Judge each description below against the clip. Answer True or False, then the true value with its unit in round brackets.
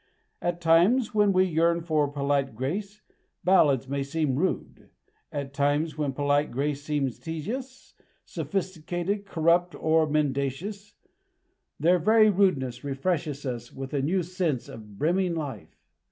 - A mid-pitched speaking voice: True (155 Hz)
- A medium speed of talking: False (130 wpm)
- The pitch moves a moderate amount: True (4.6 semitones)